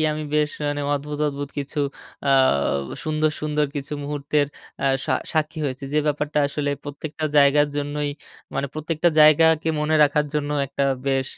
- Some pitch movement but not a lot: No, narrow, 1.2 semitones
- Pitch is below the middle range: No, medium, 150 Hz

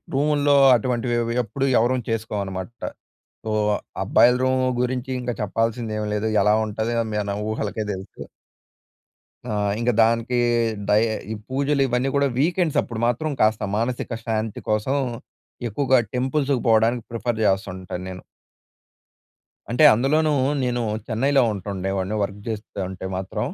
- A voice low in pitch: Yes, low, 115 Hz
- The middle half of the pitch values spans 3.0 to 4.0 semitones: Yes, average, 3.6 semitones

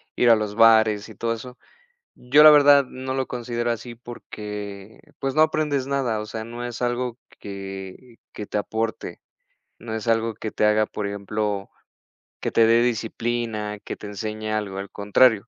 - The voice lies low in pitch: Yes, low, 115 Hz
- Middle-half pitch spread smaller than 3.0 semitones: Yes, narrow, 2.6 semitones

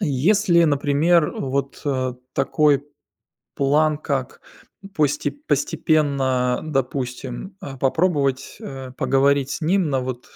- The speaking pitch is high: No, medium, 140 Hz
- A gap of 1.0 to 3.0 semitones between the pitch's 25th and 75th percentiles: Yes, narrow, 2.6 semitones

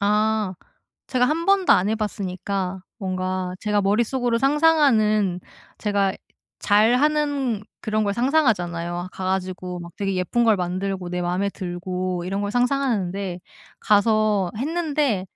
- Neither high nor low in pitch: No, high, 205 Hz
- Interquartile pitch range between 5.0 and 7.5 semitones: No, average, 4.5 semitones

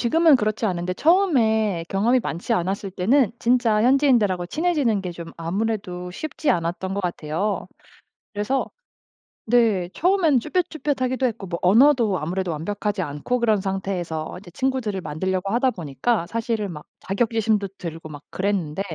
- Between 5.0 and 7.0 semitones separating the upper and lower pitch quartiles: Yes, average, 5.3 semitones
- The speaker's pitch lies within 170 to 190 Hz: No, high, 205 Hz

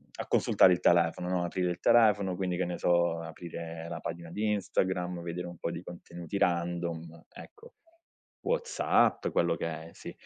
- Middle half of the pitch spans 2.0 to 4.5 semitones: No, narrow, 1.5 semitones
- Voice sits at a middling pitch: No, very low, 90 Hz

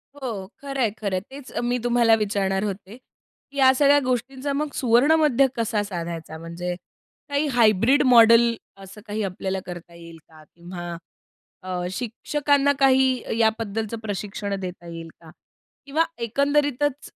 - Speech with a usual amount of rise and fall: No, wide, 5.8 semitones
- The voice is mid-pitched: No, high, 225 Hz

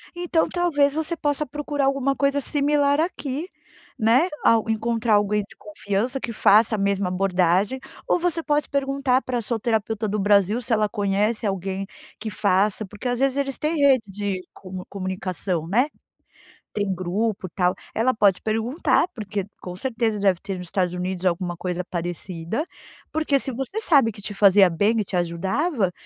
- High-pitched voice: Yes, high, 215 Hz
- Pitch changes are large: Yes, wide, 6.0 semitones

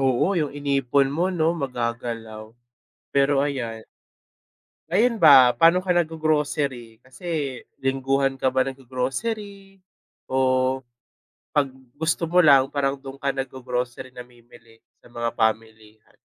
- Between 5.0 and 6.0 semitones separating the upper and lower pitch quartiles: No, average, 3.5 semitones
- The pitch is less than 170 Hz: Yes, low, 135 Hz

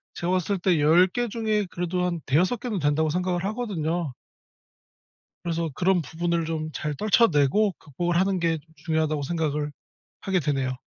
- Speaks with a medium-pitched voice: Yes, medium, 170 Hz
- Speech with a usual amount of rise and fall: Yes, average, 3.2 semitones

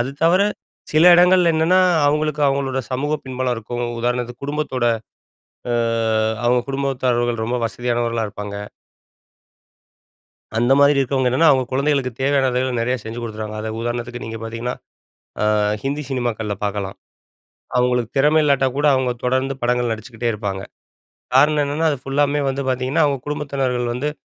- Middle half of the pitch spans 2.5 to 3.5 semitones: Yes, average, 2.9 semitones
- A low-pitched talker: Yes, low, 130 Hz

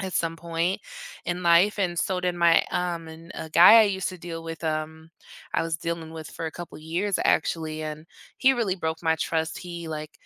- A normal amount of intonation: No, narrow, 1.9 semitones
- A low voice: No, medium, 165 Hz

